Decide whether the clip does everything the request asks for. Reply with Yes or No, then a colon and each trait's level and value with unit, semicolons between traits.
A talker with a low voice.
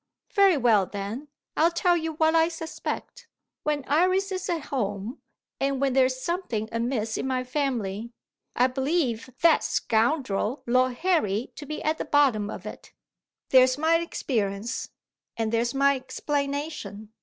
No: very high, 265 Hz